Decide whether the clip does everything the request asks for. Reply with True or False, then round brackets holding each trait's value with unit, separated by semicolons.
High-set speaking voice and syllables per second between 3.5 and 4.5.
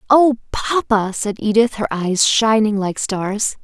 True (220 Hz; 3.8 syllables/s)